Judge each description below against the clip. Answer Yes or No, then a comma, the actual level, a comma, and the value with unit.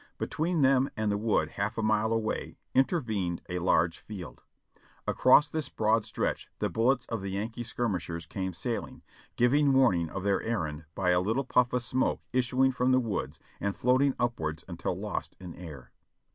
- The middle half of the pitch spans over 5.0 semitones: Yes, wide, 5.6 semitones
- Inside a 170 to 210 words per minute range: Yes, average, 175 wpm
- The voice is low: Yes, low, 110 Hz